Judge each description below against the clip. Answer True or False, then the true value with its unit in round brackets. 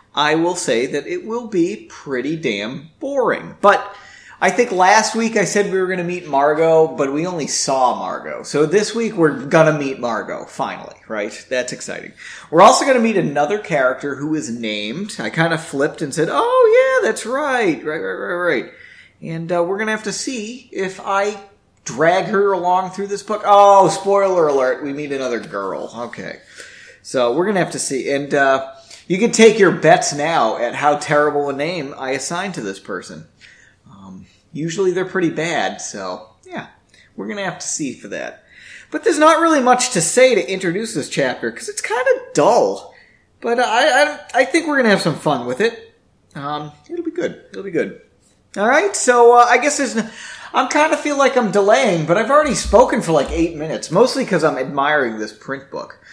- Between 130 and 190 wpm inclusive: False (205 wpm)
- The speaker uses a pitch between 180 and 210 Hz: True (185 Hz)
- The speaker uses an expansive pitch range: True (8.0 semitones)